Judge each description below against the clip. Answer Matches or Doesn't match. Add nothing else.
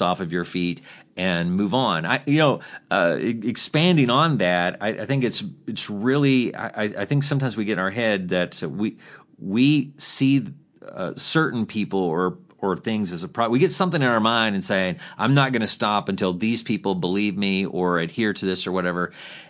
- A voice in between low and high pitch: Doesn't match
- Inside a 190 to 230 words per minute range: Matches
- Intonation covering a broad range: Matches